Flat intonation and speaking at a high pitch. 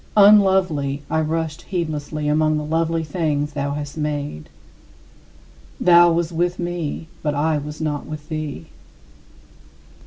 No: narrow, 2.2 semitones; medium, 155 Hz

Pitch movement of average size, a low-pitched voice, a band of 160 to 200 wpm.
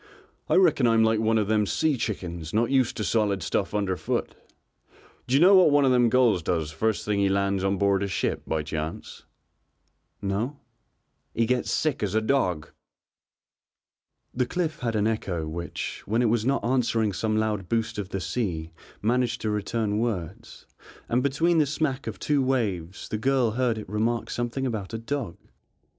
Yes: average, 4.3 semitones; low, 110 Hz; average, 180 wpm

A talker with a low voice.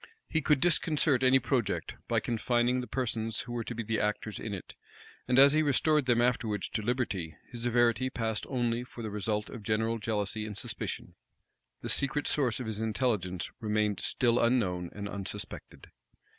Yes: low, 115 Hz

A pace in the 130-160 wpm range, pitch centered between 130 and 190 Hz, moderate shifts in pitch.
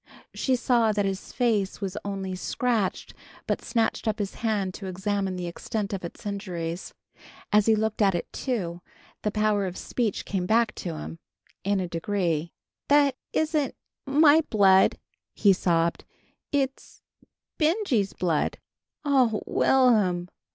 No: average, 150 wpm; high, 205 Hz; average, 4.3 semitones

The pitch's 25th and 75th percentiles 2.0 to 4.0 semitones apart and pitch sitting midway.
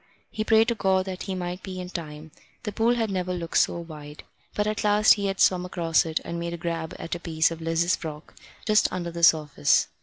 Yes: average, 2.9 semitones; medium, 175 Hz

